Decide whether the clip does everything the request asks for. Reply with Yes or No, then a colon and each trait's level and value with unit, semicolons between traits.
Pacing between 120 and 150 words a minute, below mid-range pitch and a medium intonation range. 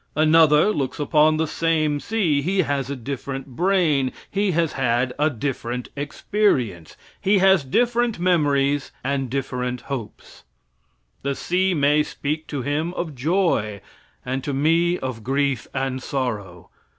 No: average, 140 wpm; medium, 145 Hz; average, 4.1 semitones